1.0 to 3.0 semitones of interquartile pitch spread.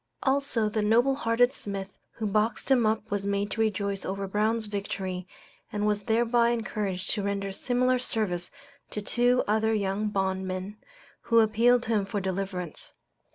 Yes: average, 2.7 semitones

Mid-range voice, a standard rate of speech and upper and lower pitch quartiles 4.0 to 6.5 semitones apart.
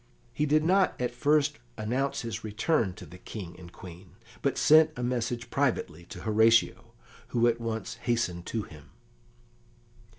No: low, 115 Hz; average, 155 wpm; average, 4.3 semitones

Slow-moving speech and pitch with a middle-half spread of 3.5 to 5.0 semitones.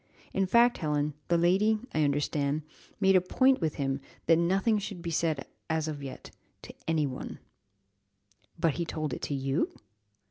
No: average, 175 wpm; average, 4.4 semitones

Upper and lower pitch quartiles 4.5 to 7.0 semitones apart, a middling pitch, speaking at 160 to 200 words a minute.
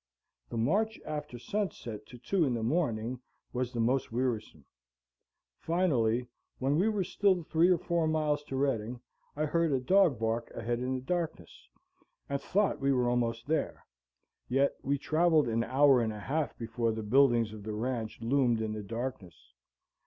No: average, 5.1 semitones; low, 130 Hz; average, 170 wpm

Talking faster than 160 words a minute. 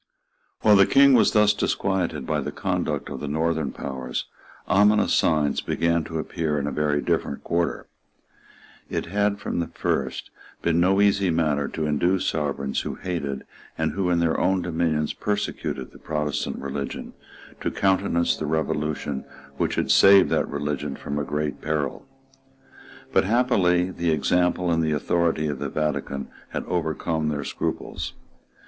No: average, 155 wpm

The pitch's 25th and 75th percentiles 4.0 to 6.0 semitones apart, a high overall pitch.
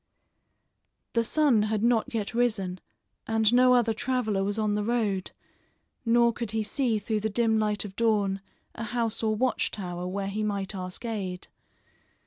No: narrow, 2.6 semitones; high, 220 Hz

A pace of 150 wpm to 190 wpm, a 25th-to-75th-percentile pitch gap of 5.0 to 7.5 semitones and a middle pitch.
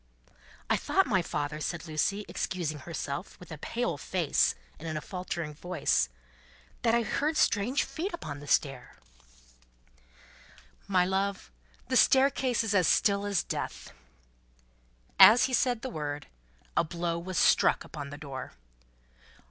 No: average, 140 wpm; wide, 5.6 semitones; medium, 180 Hz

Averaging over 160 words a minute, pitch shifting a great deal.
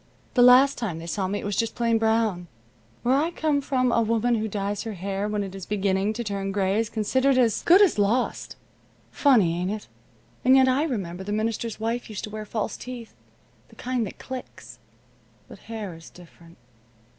No: average, 200 wpm; average, 3.8 semitones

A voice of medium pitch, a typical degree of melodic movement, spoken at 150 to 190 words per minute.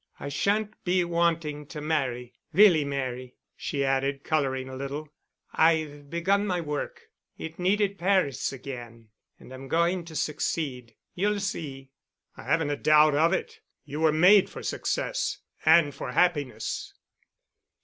No: medium, 150 Hz; average, 4.0 semitones; slow, 135 wpm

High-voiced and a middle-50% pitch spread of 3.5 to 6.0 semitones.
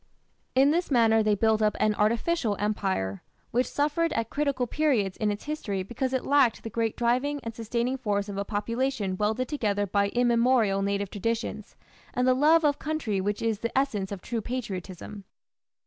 Yes: high, 225 Hz; average, 4.1 semitones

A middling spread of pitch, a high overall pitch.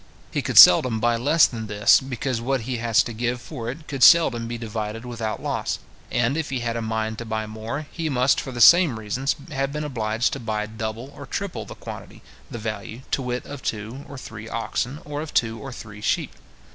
No: average, 3.5 semitones; low, 120 Hz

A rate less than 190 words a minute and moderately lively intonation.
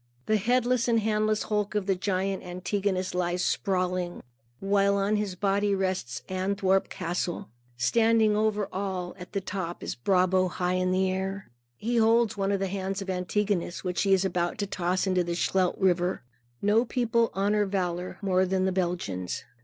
No: average, 170 wpm; narrow, 2.2 semitones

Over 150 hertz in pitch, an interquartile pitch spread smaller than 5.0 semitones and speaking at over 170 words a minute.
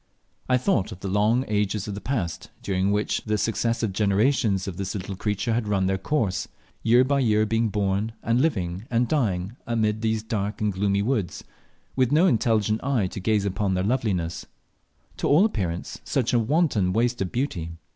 No: low, 105 Hz; average, 3.5 semitones; average, 185 wpm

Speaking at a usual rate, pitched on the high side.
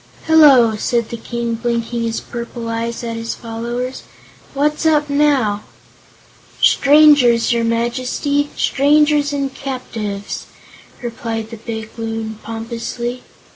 No: slow, 110 wpm; high, 235 Hz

